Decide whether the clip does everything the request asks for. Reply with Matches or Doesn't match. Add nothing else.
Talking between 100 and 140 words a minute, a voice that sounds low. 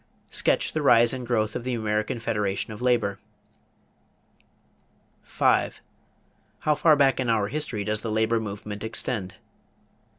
Matches